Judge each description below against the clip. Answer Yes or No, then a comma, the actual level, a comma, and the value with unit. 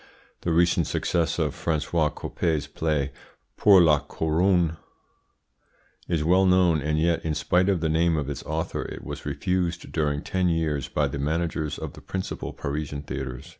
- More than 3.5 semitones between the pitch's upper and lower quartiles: No, narrow, 2.5 semitones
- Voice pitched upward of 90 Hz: No, very low, 80 Hz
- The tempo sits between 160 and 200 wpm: Yes, average, 165 wpm